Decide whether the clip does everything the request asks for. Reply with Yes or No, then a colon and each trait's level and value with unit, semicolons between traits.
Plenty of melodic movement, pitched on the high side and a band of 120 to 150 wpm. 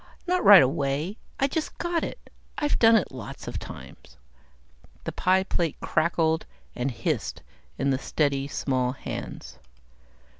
No: wide, 8.0 semitones; medium, 160 Hz; average, 140 wpm